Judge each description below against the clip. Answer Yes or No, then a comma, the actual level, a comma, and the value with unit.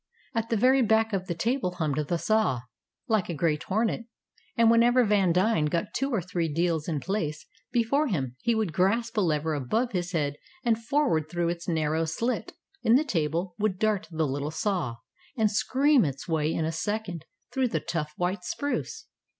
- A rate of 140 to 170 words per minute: No, average, 185 wpm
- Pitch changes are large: Yes, wide, 6.0 semitones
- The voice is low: No, medium, 185 Hz